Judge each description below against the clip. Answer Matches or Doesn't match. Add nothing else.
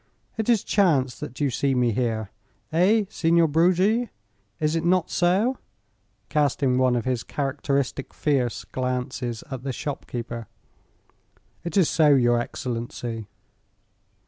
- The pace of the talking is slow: Matches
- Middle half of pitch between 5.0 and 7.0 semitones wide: Matches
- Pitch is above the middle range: Doesn't match